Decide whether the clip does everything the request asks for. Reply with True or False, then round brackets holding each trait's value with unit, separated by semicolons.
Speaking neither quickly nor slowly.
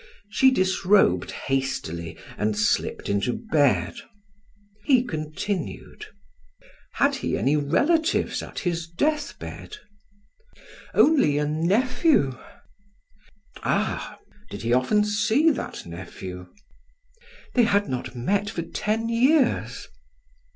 False (100 wpm)